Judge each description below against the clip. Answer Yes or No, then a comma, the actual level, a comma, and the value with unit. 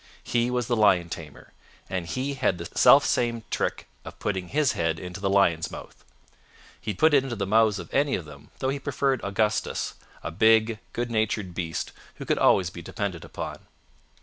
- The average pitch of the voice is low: Yes, low, 105 Hz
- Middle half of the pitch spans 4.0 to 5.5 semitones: Yes, average, 5.1 semitones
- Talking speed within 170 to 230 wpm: Yes, average, 190 wpm